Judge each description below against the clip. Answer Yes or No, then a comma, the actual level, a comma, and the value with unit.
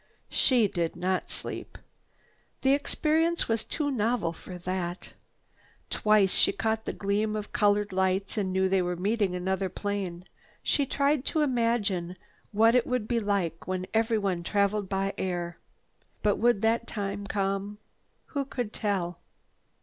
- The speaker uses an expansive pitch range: No, average, 3.4 semitones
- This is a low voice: No, high, 205 Hz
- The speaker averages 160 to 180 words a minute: No, average, 145 wpm